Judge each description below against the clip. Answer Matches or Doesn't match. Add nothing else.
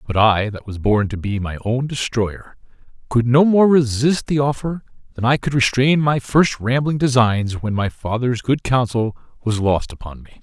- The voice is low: Matches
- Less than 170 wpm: Doesn't match